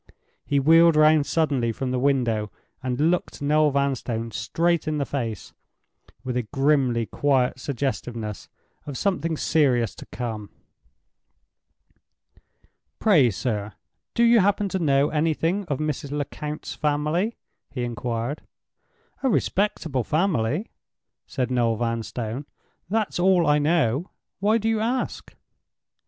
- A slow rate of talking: Yes, slow, 120 wpm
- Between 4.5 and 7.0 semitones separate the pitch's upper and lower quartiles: Yes, average, 5.2 semitones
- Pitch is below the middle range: No, medium, 145 Hz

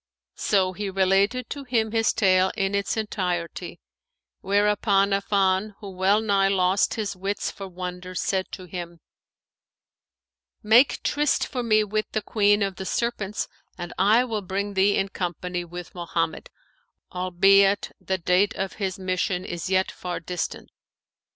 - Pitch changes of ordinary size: No, narrow, 2.2 semitones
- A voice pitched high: Yes, high, 195 Hz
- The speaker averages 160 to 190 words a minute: No, average, 145 wpm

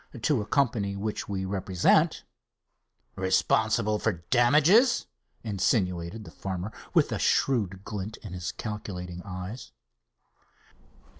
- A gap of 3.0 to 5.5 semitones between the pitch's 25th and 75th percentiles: Yes, average, 3.5 semitones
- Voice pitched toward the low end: Yes, low, 100 Hz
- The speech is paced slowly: Yes, slow, 105 wpm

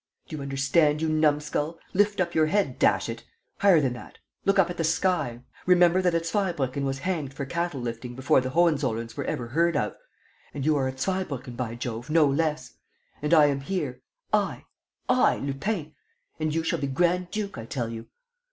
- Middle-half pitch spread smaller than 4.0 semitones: No, average, 4.6 semitones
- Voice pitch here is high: No, medium, 150 Hz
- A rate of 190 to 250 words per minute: Yes, average, 195 wpm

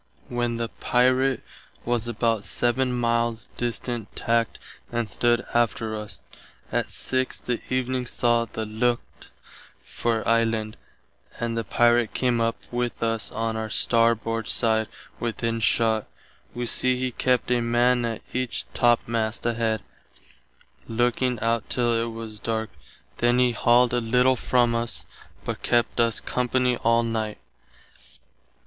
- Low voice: Yes, low, 115 Hz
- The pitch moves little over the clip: Yes, narrow, 1.2 semitones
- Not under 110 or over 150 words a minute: Yes, slow, 135 wpm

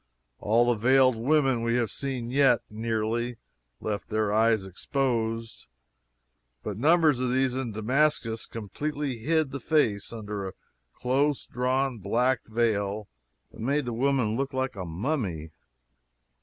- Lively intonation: No, average, 3.5 semitones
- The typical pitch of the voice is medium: No, low, 120 Hz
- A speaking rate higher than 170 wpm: No, slow, 135 wpm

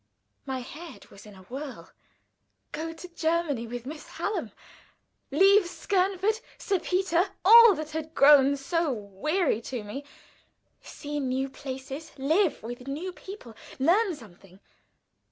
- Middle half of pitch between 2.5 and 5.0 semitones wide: No, wide, 5.6 semitones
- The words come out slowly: Yes, slow, 130 wpm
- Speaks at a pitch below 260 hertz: No, very high, 300 Hz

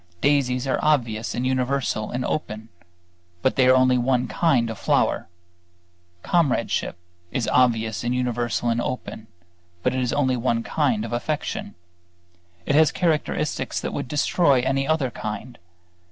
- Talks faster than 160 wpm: No, average, 145 wpm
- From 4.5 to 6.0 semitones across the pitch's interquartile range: No, average, 2.7 semitones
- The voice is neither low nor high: No, low, 125 Hz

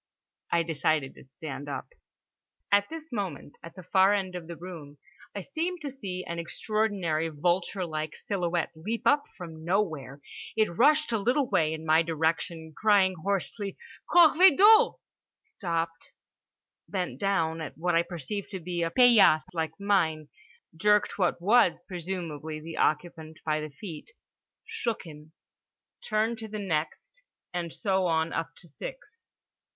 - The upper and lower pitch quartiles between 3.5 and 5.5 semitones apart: Yes, average, 4.5 semitones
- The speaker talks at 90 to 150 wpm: Yes, average, 145 wpm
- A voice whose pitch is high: No, medium, 175 Hz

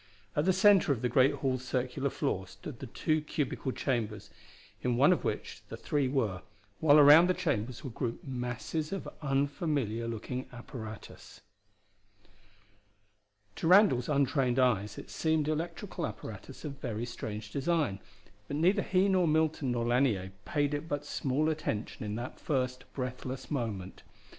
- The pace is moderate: Yes, average, 150 wpm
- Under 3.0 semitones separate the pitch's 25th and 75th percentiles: No, average, 4.3 semitones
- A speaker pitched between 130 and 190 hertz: Yes, low, 135 Hz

